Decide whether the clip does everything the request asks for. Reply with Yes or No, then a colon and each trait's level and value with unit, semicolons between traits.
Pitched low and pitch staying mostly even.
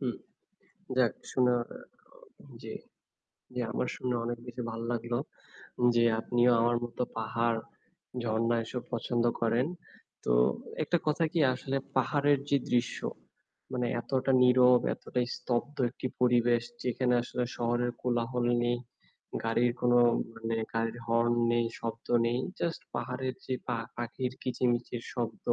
Yes: low, 120 Hz; narrow, 1.3 semitones